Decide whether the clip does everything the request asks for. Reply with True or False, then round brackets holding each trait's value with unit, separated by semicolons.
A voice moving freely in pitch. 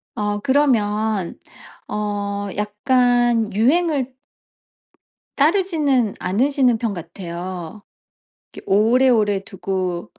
False (4.3 semitones)